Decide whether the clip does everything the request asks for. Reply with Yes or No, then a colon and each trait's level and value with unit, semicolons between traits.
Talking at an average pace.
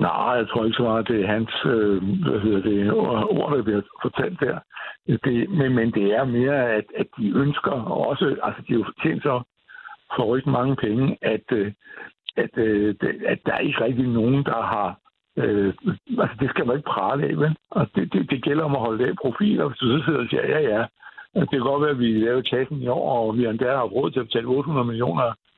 No: fast, 230 wpm